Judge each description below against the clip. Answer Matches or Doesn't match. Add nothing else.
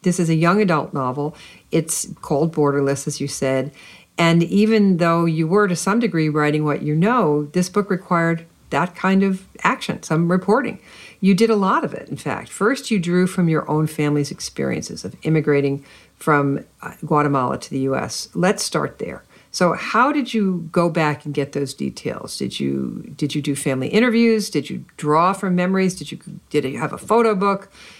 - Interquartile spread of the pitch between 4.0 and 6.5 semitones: Matches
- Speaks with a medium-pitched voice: Matches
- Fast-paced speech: Doesn't match